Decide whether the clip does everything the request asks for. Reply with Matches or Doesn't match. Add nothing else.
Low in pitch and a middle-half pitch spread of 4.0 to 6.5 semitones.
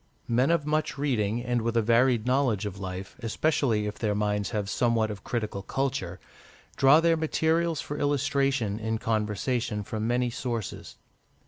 Matches